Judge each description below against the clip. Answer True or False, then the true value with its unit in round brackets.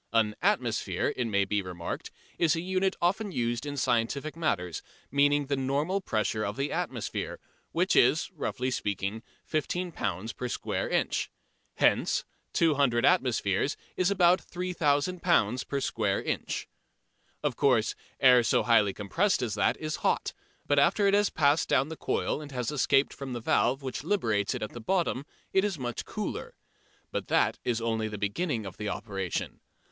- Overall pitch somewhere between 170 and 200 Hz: False (130 Hz)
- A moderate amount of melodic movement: False (6.5 semitones)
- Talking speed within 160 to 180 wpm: True (165 wpm)